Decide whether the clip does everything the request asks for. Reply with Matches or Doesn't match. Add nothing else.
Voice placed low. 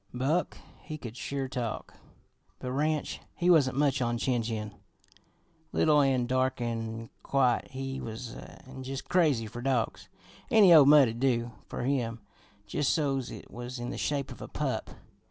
Matches